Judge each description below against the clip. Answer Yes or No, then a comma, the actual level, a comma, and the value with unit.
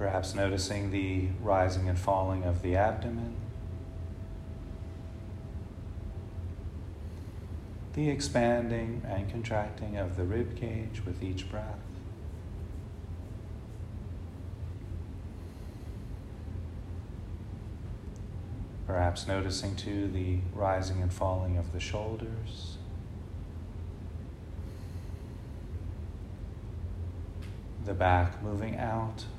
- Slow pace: Yes, slow, 70 wpm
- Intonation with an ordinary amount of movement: No, narrow, 2.3 semitones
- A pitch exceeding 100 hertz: No, very low, 95 Hz